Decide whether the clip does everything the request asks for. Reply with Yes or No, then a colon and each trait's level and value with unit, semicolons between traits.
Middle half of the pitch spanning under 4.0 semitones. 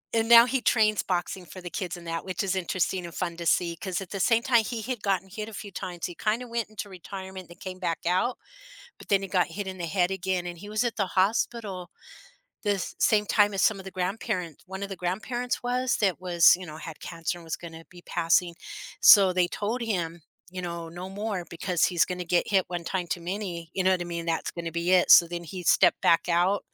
Yes: average, 2.8 semitones